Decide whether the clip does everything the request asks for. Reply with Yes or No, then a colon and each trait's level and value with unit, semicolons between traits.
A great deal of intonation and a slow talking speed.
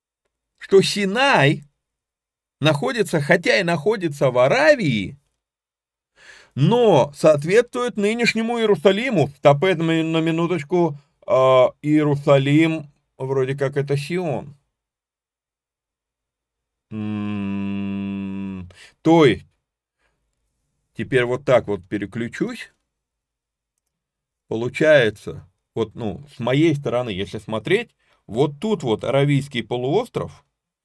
Yes: wide, 7.8 semitones; slow, 80 wpm